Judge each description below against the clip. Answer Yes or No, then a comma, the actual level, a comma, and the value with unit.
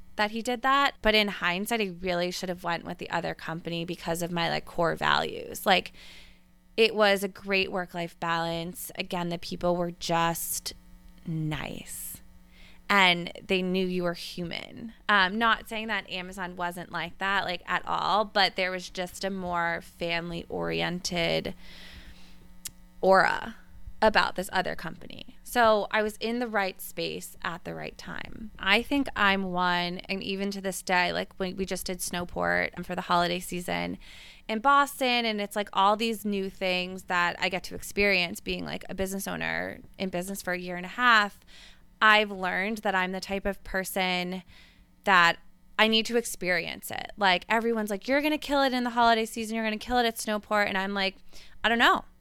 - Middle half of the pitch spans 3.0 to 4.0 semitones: Yes, average, 3.4 semitones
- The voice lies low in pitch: No, medium, 185 Hz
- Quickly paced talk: No, average, 185 wpm